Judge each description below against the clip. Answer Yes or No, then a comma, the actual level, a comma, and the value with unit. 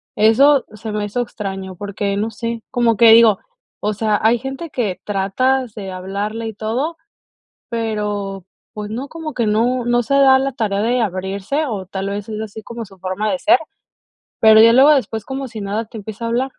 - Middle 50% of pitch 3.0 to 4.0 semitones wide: Yes, average, 3.3 semitones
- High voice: Yes, high, 220 Hz